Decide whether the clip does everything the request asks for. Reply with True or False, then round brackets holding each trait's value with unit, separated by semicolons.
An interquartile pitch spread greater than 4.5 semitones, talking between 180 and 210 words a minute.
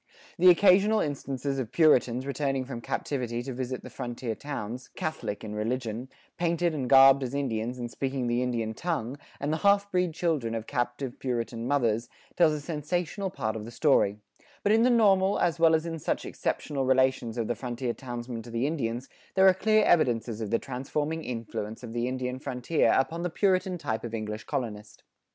True (5.4 semitones; 185 wpm)